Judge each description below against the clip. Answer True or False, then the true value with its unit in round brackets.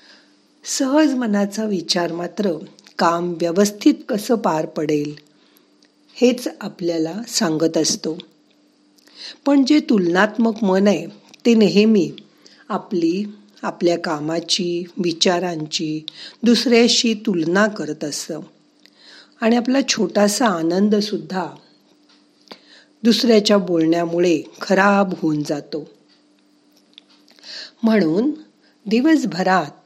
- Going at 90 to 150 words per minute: False (80 wpm)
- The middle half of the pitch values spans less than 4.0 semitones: False (5.3 semitones)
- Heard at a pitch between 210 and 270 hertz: False (200 Hz)